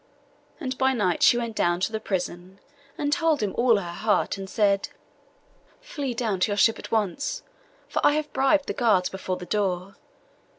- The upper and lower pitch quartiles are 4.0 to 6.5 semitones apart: Yes, wide, 5.6 semitones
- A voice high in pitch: Yes, high, 215 Hz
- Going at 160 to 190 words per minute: Yes, average, 185 wpm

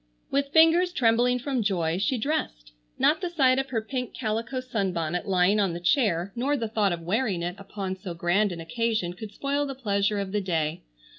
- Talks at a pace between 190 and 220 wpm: Yes, average, 200 wpm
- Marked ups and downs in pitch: Yes, wide, 6.1 semitones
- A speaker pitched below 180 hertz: No, high, 215 Hz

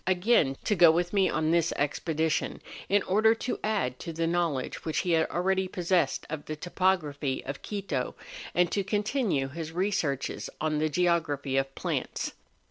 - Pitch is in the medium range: Yes, medium, 170 Hz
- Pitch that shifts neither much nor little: Yes, average, 4.0 semitones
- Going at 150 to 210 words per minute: Yes, average, 165 wpm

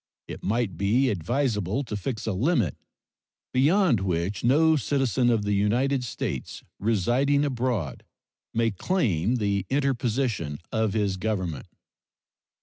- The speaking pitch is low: Yes, low, 115 Hz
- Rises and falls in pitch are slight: No, average, 5.0 semitones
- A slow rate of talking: Yes, slow, 120 wpm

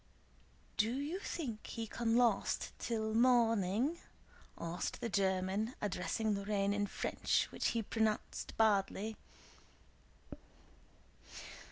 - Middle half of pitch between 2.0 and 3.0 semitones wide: Yes, average, 2.7 semitones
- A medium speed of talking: No, slow, 95 wpm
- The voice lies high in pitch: Yes, high, 220 Hz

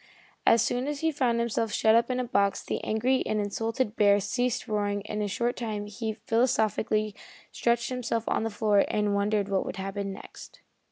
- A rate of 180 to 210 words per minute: Yes, average, 200 wpm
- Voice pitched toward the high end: Yes, high, 220 Hz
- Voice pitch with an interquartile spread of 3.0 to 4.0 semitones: No, narrow, 2.5 semitones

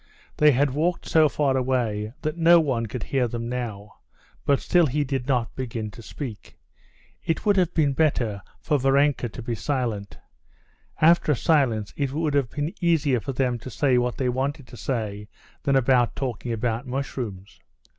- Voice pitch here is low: Yes, low, 130 Hz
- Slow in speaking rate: No, average, 175 wpm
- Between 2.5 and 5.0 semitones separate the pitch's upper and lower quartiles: Yes, average, 3.8 semitones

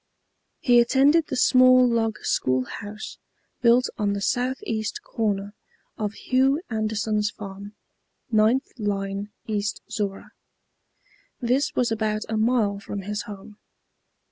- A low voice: No, high, 215 Hz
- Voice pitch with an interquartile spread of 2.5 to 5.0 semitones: Yes, average, 3.2 semitones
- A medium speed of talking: No, slow, 120 wpm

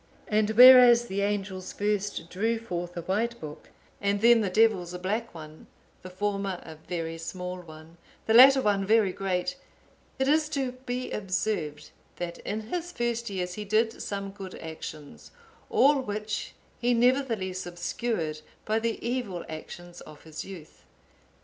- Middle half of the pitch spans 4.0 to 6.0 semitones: Yes, average, 4.6 semitones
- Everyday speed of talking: Yes, average, 155 wpm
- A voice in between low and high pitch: No, high, 200 Hz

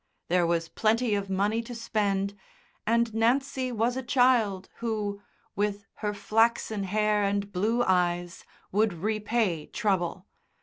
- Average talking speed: No, slow, 130 wpm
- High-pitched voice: Yes, high, 210 Hz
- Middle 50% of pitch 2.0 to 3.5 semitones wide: Yes, average, 2.9 semitones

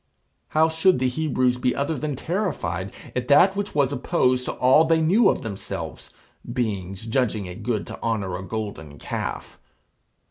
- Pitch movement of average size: No, wide, 7.6 semitones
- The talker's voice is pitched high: No, low, 125 Hz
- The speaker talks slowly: No, average, 165 wpm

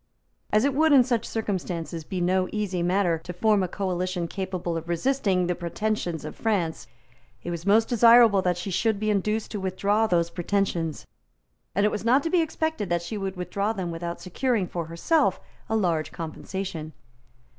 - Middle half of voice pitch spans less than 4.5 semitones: Yes, average, 4.0 semitones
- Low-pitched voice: No, high, 190 Hz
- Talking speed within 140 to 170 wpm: No, average, 180 wpm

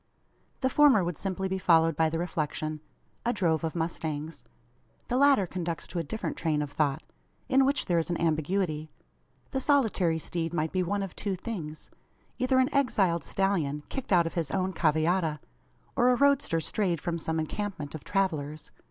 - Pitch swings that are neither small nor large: Yes, average, 4.3 semitones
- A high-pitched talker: No, medium, 170 Hz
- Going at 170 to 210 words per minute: Yes, average, 180 wpm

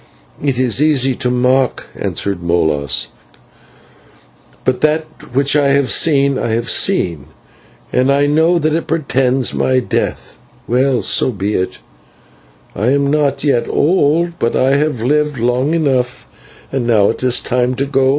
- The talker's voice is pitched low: Yes, low, 130 Hz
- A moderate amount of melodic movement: Yes, average, 3.0 semitones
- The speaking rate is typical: Yes, average, 150 wpm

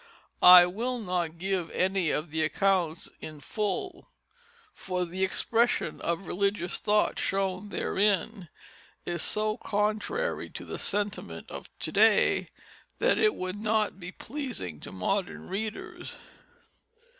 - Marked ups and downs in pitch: No, average, 3.1 semitones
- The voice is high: Yes, high, 195 Hz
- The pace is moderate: No, slow, 125 wpm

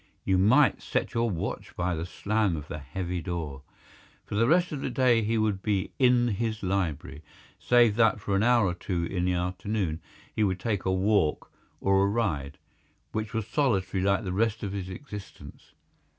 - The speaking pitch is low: Yes, low, 100 Hz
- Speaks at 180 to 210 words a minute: Yes, average, 185 wpm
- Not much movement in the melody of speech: No, average, 3.7 semitones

